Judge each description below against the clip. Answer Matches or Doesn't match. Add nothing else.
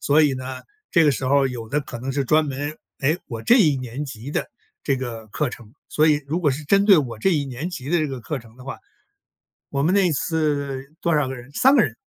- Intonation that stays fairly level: Doesn't match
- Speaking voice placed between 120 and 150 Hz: Matches